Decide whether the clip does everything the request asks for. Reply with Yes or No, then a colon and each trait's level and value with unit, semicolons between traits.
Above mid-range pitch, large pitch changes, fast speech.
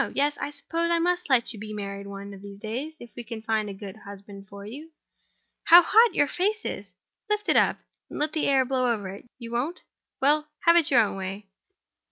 Yes: high, 240 Hz; wide, 7.2 semitones; fast, 210 wpm